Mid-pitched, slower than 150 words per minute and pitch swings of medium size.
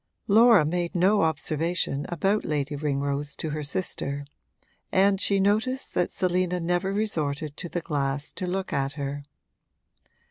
Yes: medium, 170 Hz; average, 140 wpm; average, 4.9 semitones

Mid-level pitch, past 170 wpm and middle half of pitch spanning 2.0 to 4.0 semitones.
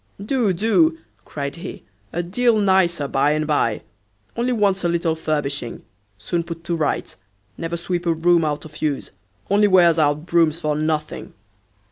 No: medium, 170 Hz; average, 160 wpm; average, 3.6 semitones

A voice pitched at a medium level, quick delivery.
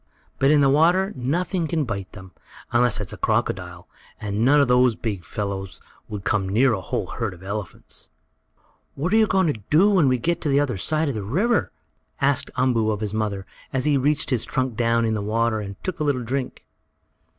No: low, 125 Hz; fast, 210 wpm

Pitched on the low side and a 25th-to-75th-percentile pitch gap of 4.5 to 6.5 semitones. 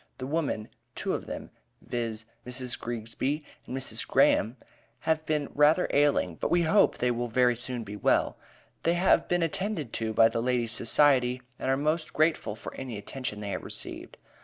Yes: low, 125 Hz; average, 4.9 semitones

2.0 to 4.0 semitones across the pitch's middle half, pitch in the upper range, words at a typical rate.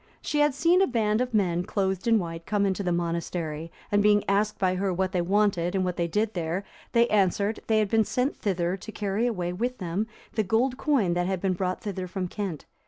No: average, 3.5 semitones; high, 195 Hz; fast, 230 wpm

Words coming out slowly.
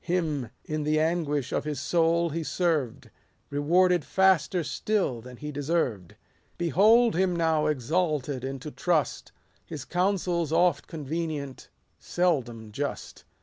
Yes: slow, 125 wpm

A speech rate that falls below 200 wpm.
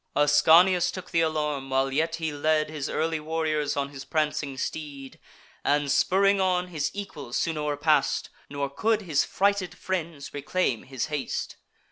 Yes: average, 150 wpm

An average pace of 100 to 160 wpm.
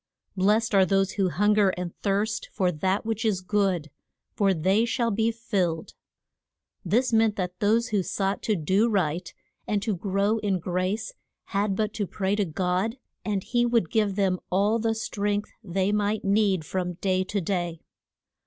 No: average, 170 wpm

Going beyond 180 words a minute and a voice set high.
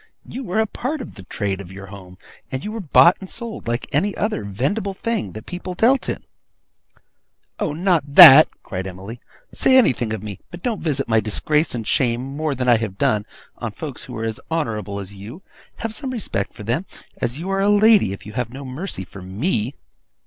No: fast, 205 wpm; low, 135 Hz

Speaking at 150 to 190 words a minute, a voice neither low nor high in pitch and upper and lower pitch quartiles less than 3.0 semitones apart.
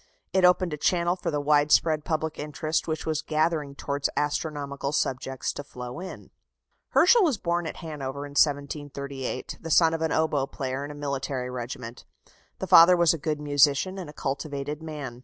Yes: average, 175 wpm; medium, 150 Hz; narrow, 2.5 semitones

